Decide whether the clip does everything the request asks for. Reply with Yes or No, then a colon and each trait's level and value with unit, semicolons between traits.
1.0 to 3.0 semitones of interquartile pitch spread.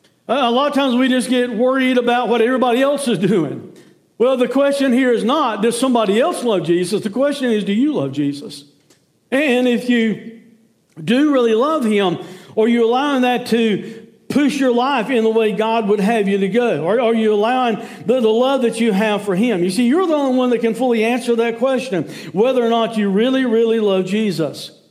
Yes: average, 2.7 semitones